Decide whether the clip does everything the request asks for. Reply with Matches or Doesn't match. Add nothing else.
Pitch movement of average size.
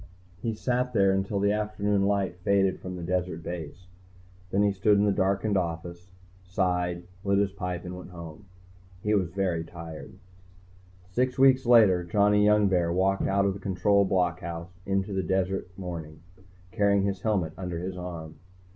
Doesn't match